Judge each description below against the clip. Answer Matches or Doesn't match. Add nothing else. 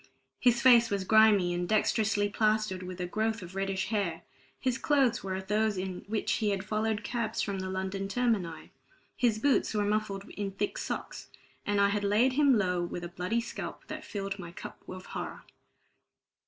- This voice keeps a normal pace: Matches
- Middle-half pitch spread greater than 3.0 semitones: Doesn't match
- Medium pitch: Doesn't match